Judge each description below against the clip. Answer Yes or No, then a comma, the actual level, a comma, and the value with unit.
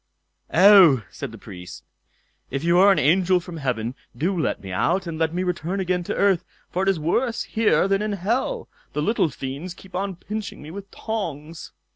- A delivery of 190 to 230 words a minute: Yes, average, 195 wpm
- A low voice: No, medium, 180 Hz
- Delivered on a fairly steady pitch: No, average, 4.2 semitones